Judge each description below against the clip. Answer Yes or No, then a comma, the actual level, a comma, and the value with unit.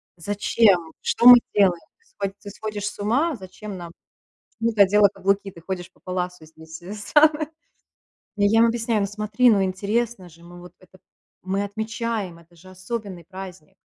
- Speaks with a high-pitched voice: Yes, high, 200 Hz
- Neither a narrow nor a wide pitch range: Yes, average, 3.3 semitones